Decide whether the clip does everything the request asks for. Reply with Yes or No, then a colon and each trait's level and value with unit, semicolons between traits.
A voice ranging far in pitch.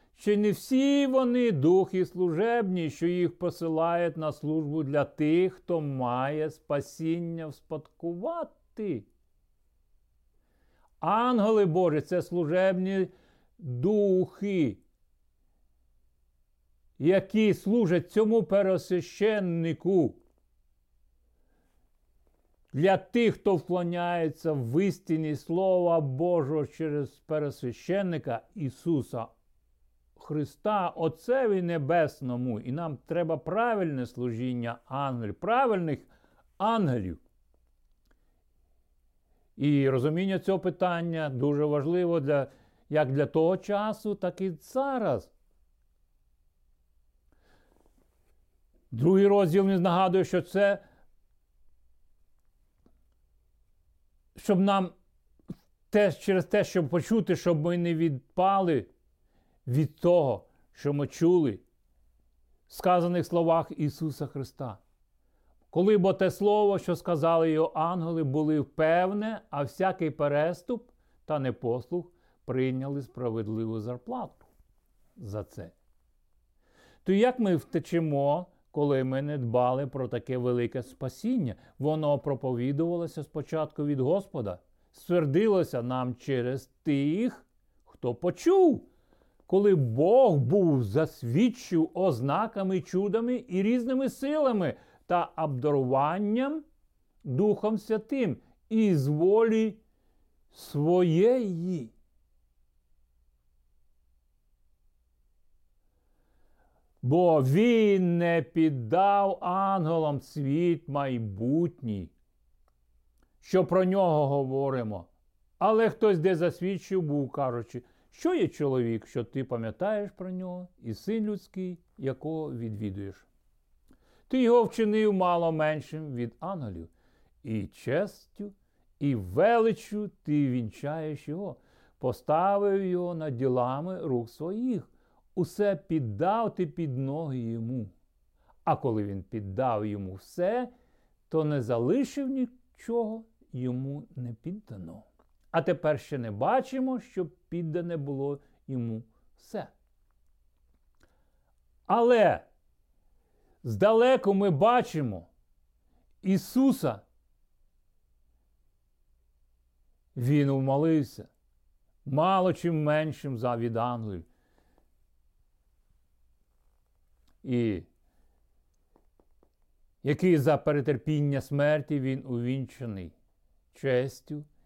Yes: wide, 8.8 semitones